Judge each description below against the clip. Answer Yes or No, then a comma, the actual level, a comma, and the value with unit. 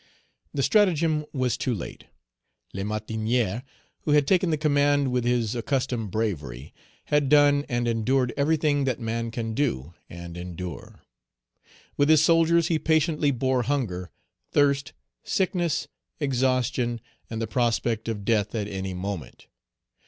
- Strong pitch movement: No, average, 4.8 semitones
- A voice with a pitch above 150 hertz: No, low, 125 Hz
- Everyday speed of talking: No, slow, 130 wpm